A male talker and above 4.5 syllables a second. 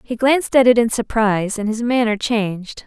No: female; 5.4 syllables/s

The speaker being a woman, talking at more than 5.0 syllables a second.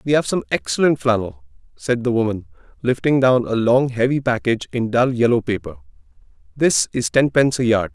No: male; 5.6 syllables/s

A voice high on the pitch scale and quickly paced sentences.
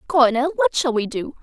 Yes: very high, 280 Hz; fast, 210 wpm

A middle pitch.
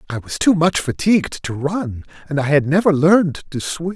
Yes: medium, 160 Hz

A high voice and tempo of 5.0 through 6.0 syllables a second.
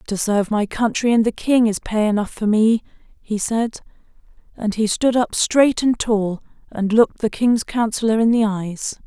No: high, 220 Hz; 4.7 syllables/s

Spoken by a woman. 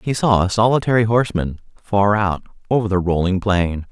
No: male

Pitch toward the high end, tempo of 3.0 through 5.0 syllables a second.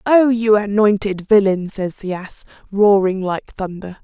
Yes: high, 200 Hz; 4.2 syllables/s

